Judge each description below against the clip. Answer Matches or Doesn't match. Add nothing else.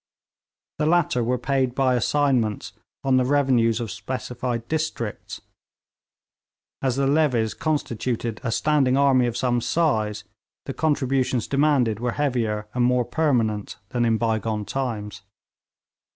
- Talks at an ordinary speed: Doesn't match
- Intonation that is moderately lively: Matches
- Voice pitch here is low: Matches